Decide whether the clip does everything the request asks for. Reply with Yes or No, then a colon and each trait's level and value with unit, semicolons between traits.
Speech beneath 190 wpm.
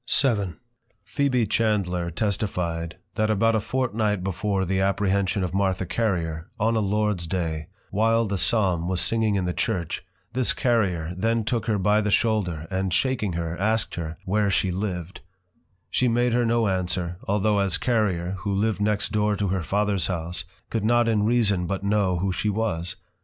Yes: average, 175 wpm